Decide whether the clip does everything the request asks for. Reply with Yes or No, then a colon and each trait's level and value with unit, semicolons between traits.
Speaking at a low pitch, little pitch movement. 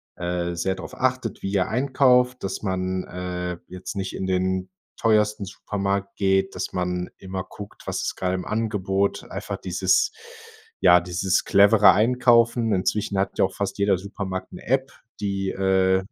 Yes: very low, 95 Hz; narrow, 2.3 semitones